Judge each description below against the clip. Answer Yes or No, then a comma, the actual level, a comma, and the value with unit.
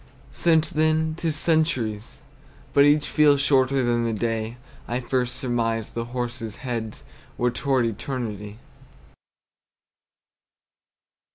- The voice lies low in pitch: Yes, low, 125 Hz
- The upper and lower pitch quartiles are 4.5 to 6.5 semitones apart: No, average, 3.9 semitones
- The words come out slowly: Yes, slow, 110 wpm